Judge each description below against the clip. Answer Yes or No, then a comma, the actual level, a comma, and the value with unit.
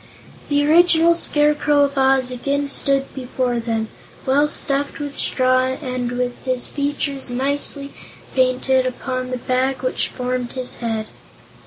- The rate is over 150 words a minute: No, slow, 135 wpm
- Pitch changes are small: Yes, narrow, 2.0 semitones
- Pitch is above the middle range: Yes, very high, 260 Hz